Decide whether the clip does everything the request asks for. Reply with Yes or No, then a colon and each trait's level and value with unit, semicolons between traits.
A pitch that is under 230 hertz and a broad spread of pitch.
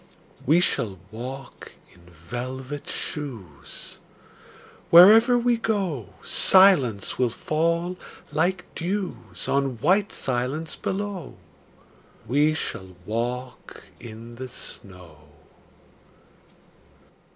Yes: low, 135 Hz; wide, 7.3 semitones